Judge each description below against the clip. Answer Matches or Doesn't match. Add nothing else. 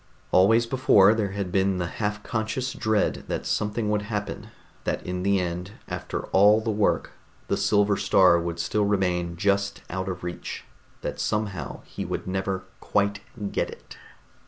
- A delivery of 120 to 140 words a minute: Doesn't match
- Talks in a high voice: Doesn't match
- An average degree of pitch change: Doesn't match